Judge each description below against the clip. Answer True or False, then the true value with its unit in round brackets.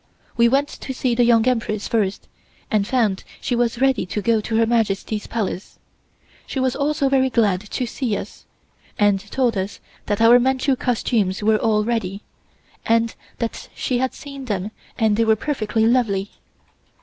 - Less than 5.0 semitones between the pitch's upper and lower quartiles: True (3.2 semitones)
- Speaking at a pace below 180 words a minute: True (170 wpm)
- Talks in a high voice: True (230 Hz)